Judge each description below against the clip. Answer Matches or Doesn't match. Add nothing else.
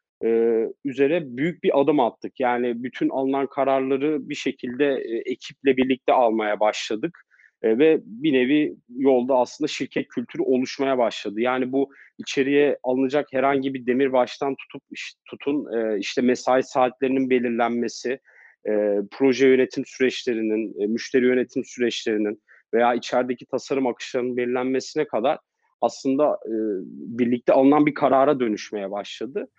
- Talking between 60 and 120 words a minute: Doesn't match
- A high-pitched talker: Doesn't match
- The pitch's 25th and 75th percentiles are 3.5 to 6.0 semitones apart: Doesn't match